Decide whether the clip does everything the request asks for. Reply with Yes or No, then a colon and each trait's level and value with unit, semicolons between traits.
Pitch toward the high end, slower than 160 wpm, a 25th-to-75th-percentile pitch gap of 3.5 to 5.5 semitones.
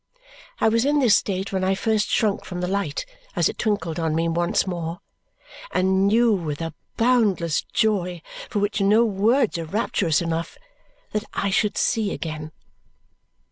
No: high, 195 Hz; average, 165 wpm; average, 4.3 semitones